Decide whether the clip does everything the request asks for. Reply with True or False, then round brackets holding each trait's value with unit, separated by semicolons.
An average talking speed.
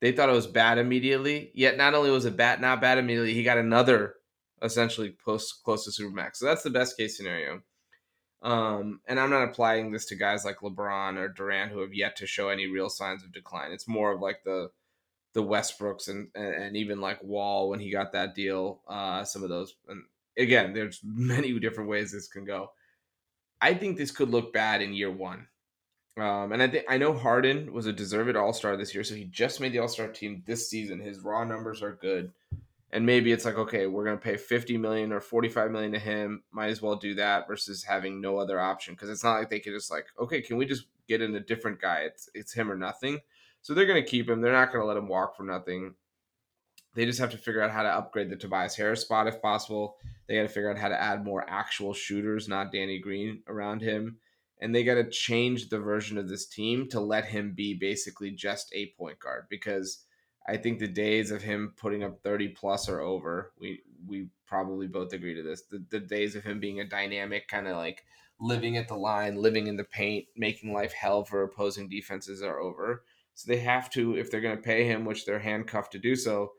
False (230 wpm)